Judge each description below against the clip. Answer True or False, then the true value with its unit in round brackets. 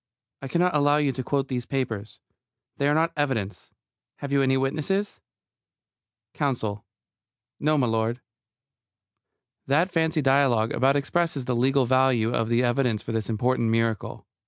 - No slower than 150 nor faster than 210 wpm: False (140 wpm)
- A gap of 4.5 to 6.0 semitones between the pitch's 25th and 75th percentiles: False (3.6 semitones)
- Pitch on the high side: False (135 Hz)